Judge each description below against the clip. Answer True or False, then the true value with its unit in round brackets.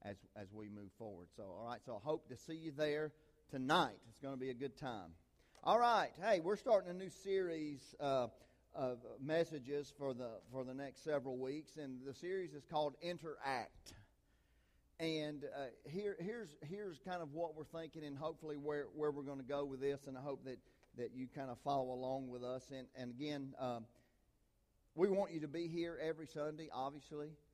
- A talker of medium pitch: True (145 Hz)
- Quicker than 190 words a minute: True (200 wpm)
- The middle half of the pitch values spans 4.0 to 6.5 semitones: False (3.5 semitones)